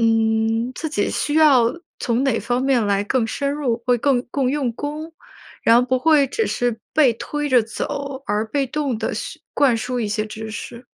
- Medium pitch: No, very high, 250 Hz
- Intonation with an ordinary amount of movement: Yes, average, 3.8 semitones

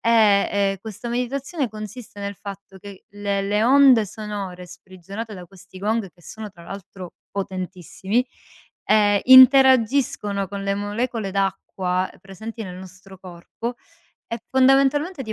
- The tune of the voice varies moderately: Yes, average, 3.4 semitones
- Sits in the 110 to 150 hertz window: No, high, 205 Hz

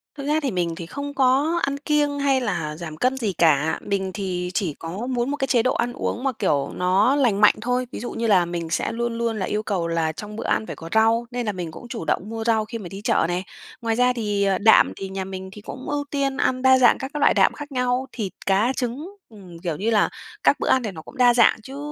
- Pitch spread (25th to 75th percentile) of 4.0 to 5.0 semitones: No, wide, 5.4 semitones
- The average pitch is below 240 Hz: Yes, high, 225 Hz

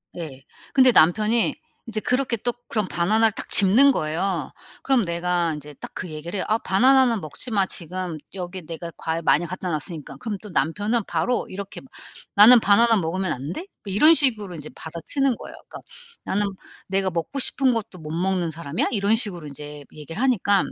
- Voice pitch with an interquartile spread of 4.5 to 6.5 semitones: Yes, wide, 5.4 semitones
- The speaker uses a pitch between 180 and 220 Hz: Yes, high, 190 Hz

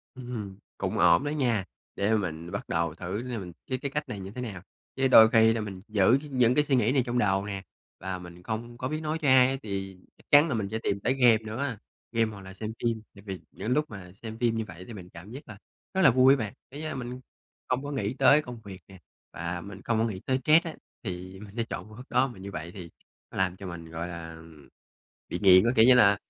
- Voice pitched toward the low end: Yes, low, 110 Hz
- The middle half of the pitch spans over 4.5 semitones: Yes, average, 5.0 semitones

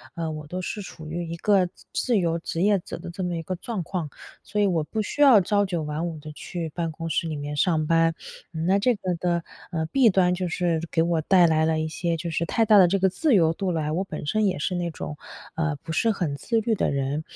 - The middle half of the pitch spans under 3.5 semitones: Yes, average, 3.1 semitones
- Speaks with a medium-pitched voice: Yes, medium, 170 Hz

